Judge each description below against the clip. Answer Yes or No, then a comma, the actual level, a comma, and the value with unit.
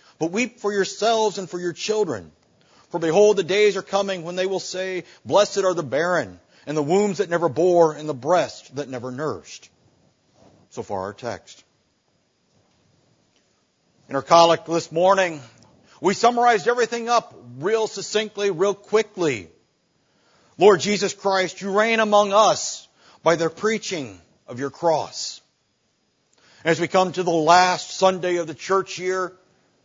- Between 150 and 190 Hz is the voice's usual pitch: Yes, medium, 185 Hz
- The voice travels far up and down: No, average, 3.9 semitones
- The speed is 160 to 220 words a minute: No, average, 150 wpm